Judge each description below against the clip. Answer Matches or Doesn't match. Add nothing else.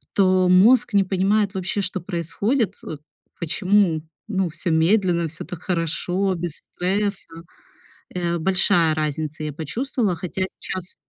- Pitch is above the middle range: Doesn't match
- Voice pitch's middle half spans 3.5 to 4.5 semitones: Doesn't match